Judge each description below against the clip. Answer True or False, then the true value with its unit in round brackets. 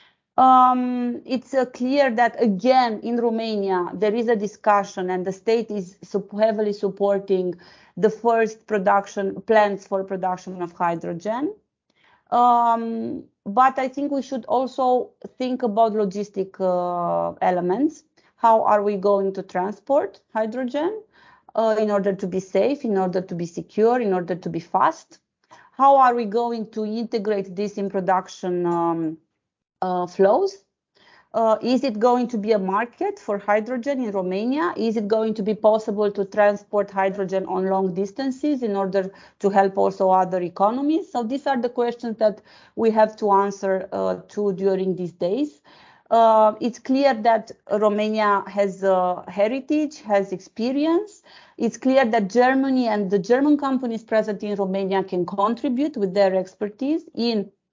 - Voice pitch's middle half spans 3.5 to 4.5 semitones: True (4.0 semitones)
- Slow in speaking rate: False (155 wpm)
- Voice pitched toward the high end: True (215 Hz)